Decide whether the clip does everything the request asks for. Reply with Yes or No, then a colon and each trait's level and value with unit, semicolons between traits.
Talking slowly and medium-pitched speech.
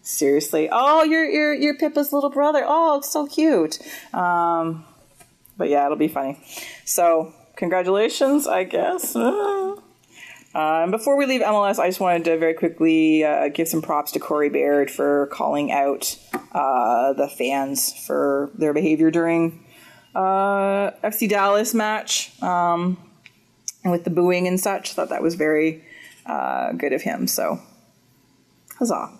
No: average, 145 wpm; medium, 175 Hz